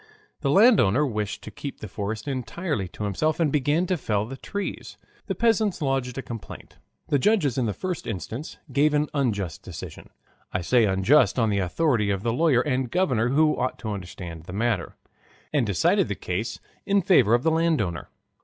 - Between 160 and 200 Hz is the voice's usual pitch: No, low, 125 Hz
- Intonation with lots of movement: Yes, wide, 6.5 semitones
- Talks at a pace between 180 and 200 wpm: Yes, average, 185 wpm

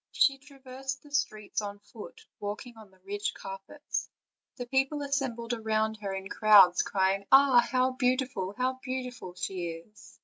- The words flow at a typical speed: Yes, average, 150 wpm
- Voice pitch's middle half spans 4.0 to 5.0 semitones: Yes, average, 4.7 semitones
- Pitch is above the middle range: Yes, high, 230 Hz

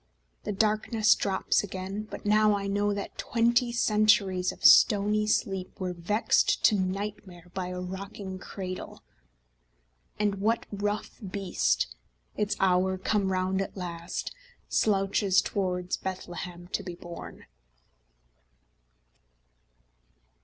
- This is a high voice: Yes, high, 195 Hz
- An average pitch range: No, narrow, 2.3 semitones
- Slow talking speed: Yes, slow, 110 wpm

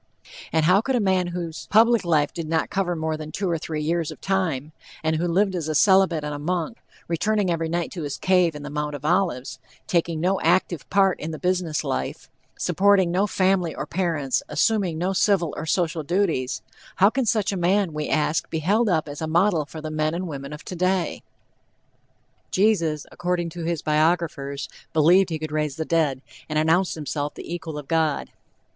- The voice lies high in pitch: No, medium, 170 Hz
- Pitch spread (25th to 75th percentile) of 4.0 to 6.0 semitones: No, average, 3.2 semitones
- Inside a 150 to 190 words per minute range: No, average, 200 wpm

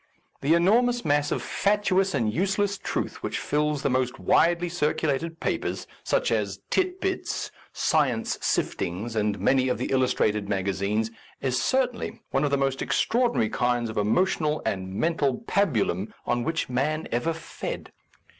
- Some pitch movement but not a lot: No, wide, 7.5 semitones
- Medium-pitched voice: Yes, medium, 145 Hz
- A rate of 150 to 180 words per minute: Yes, average, 160 wpm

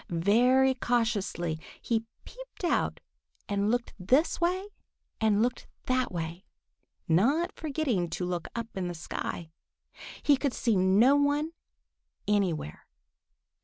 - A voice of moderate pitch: No, high, 230 Hz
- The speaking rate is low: Yes, slow, 120 wpm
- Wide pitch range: Yes, wide, 6.9 semitones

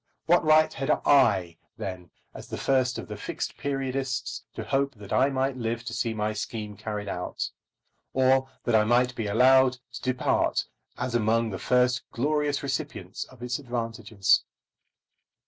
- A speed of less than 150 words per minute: No, average, 160 wpm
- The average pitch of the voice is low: Yes, low, 125 Hz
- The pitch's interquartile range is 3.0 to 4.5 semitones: Yes, average, 3.5 semitones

